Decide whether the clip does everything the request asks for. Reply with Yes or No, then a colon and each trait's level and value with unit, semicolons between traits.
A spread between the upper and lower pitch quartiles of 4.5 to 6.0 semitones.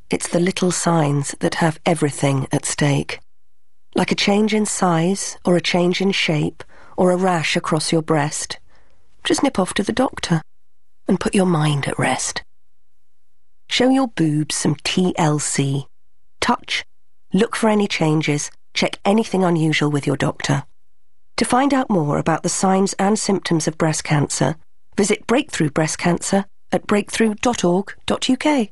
Yes: average, 4.8 semitones